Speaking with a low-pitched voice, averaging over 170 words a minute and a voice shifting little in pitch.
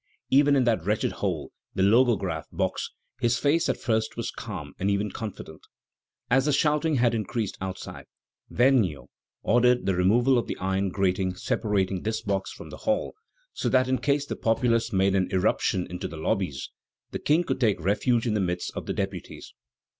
No: low, 110 Hz; average, 180 wpm; average, 4.7 semitones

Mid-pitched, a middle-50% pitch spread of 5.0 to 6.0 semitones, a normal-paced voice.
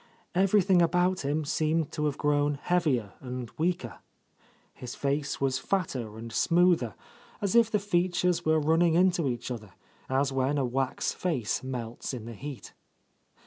Yes: medium, 145 Hz; wide, 5.4 semitones; average, 155 wpm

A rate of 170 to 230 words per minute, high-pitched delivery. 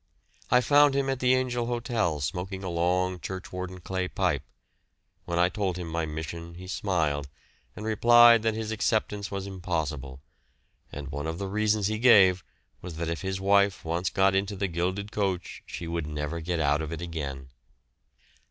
No: average, 175 wpm; very low, 90 Hz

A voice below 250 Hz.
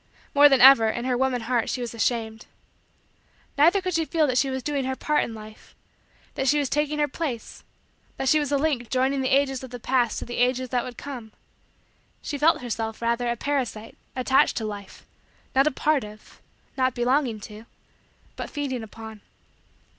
No: very high, 255 Hz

